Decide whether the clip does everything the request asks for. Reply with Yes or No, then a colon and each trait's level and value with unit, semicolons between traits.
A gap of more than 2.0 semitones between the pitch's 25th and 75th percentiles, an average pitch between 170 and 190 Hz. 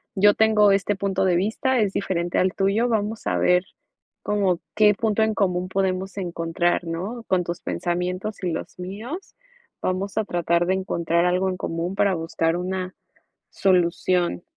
Yes: average, 2.7 semitones; medium, 185 Hz